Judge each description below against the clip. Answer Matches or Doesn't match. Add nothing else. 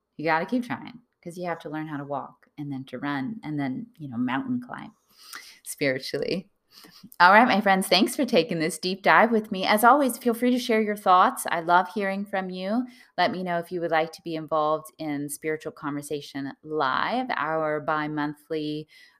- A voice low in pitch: Doesn't match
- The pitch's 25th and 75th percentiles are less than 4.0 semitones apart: Doesn't match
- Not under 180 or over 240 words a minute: Matches